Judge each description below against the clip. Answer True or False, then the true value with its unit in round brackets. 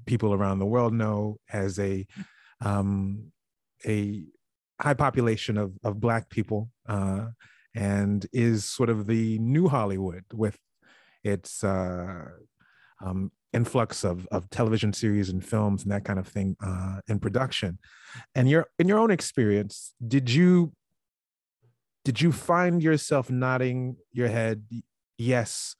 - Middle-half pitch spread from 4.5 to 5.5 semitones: False (3.9 semitones)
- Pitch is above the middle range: False (110 Hz)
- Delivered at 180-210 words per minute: False (135 wpm)